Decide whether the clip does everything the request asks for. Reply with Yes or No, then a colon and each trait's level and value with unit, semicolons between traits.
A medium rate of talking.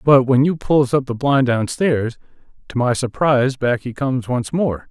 Yes: average, 195 wpm